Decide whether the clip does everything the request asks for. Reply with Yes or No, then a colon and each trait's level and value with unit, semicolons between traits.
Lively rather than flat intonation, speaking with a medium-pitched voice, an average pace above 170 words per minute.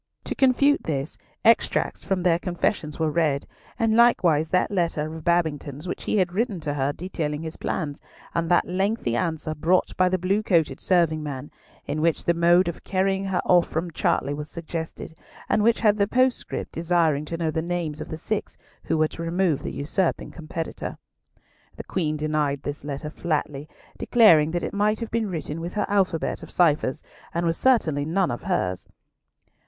No: average, 3.5 semitones; medium, 170 Hz; average, 185 wpm